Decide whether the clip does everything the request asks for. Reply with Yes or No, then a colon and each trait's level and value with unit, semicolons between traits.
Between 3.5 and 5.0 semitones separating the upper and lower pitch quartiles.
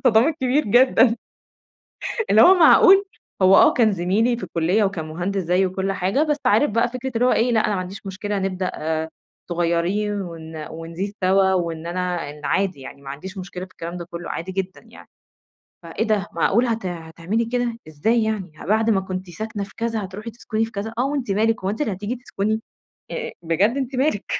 Yes: average, 4.1 semitones